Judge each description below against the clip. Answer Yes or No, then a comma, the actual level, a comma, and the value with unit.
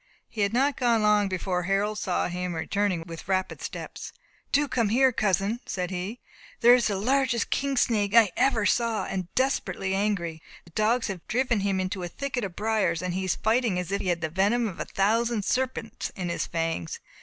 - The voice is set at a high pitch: Yes, high, 205 Hz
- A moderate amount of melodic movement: Yes, average, 4.3 semitones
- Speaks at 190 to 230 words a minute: Yes, average, 200 wpm